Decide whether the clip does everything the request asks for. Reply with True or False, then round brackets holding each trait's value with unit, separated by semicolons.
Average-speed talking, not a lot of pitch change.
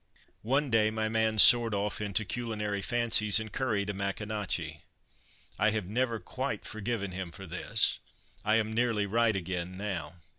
True (155 wpm; 2.3 semitones)